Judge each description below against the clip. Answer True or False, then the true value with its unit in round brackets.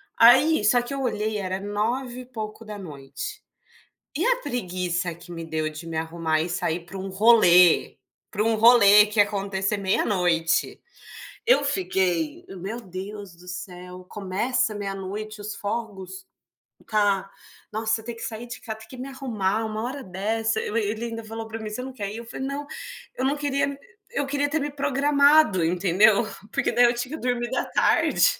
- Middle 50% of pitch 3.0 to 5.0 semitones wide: True (4.5 semitones)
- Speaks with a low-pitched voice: False (215 Hz)